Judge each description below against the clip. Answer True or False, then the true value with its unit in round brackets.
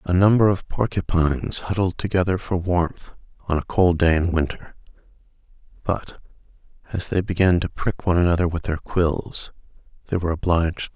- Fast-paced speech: False (165 wpm)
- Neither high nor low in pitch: False (85 Hz)